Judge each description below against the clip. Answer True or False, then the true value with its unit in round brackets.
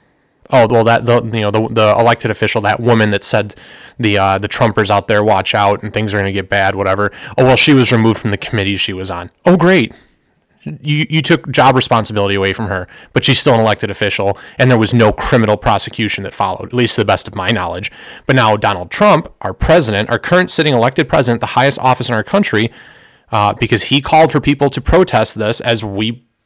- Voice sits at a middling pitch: False (115 Hz)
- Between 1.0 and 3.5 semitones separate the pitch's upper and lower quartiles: False (3.9 semitones)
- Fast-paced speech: True (230 wpm)